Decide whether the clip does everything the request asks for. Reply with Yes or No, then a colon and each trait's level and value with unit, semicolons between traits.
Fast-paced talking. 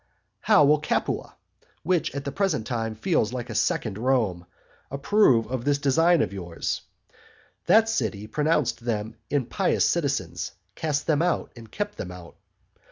No: average, 150 wpm